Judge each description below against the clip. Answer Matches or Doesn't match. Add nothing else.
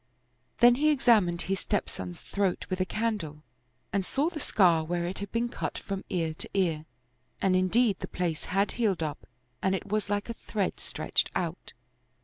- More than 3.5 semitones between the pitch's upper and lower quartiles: Matches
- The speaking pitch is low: Doesn't match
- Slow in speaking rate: Doesn't match